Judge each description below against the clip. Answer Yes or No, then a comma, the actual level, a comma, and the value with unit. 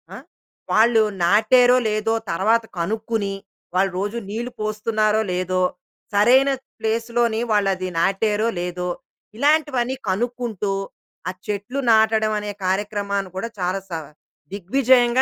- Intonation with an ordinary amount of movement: Yes, average, 3.2 semitones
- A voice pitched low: No, high, 215 Hz